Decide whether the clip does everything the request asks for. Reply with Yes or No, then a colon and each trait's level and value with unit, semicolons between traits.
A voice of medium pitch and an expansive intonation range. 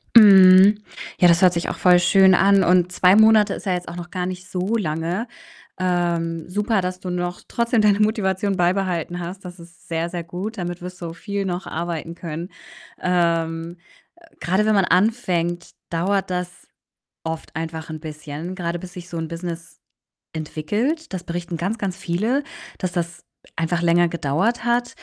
No: medium, 180 Hz; narrow, 2.4 semitones